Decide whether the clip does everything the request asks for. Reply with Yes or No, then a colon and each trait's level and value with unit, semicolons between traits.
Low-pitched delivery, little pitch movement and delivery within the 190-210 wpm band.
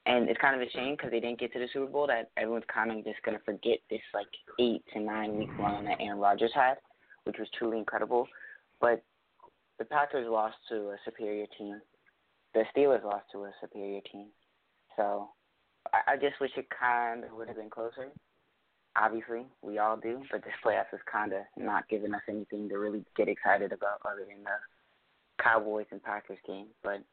Yes: low, 110 Hz; narrow, 2.2 semitones; average, 200 wpm